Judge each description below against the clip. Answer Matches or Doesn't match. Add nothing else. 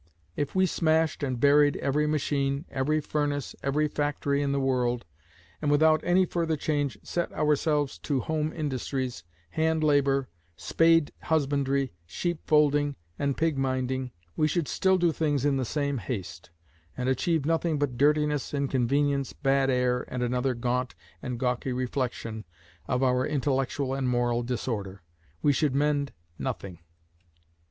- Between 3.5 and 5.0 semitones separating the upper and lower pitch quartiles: Doesn't match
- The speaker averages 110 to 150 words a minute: Matches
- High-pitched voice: Doesn't match